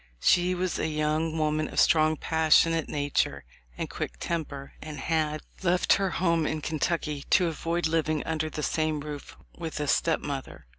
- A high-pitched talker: No, medium, 155 Hz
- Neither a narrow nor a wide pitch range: No, narrow, 1.5 semitones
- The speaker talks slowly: No, average, 160 wpm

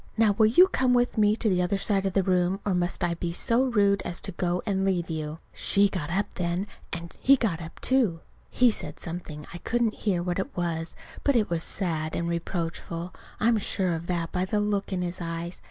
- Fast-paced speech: Yes, fast, 225 wpm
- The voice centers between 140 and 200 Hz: Yes, medium, 185 Hz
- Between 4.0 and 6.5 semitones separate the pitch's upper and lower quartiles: No, average, 3.4 semitones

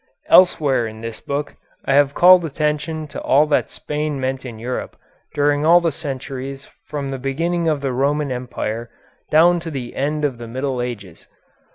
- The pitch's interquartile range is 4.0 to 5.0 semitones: No, average, 3.0 semitones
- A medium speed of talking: Yes, average, 175 wpm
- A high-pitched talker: No, medium, 140 Hz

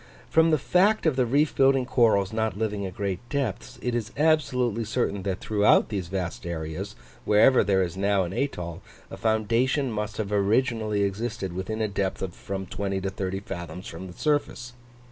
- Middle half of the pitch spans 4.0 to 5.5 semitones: Yes, average, 4.3 semitones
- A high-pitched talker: No, low, 105 Hz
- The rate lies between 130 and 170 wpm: No, average, 185 wpm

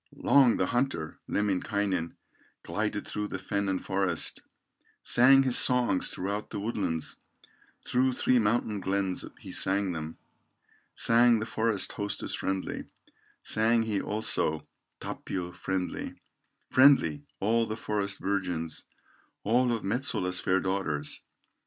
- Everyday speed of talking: No, slow, 120 wpm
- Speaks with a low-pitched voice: Yes, low, 100 Hz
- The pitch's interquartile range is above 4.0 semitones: No, average, 3.7 semitones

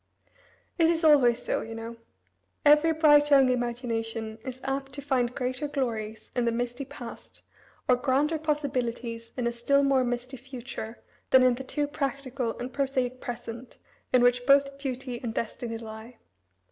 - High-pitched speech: Yes, very high, 255 Hz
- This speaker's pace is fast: No, average, 160 wpm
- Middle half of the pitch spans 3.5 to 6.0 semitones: No, average, 2.7 semitones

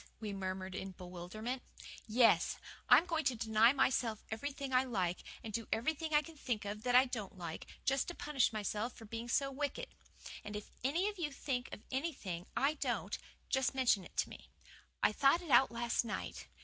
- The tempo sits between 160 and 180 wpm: No, average, 190 wpm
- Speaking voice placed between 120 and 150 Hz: No, high, 245 Hz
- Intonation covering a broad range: No, average, 4.7 semitones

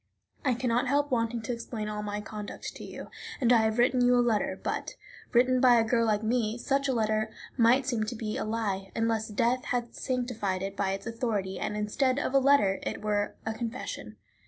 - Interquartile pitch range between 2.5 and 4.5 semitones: Yes, average, 2.8 semitones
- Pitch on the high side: Yes, high, 230 Hz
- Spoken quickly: Yes, fast, 215 wpm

